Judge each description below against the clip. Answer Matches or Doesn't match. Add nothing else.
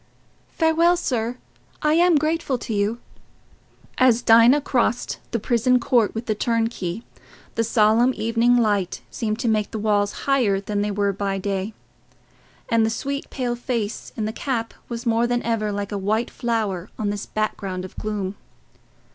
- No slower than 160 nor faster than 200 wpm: Matches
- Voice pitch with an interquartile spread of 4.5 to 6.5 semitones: Doesn't match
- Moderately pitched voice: Doesn't match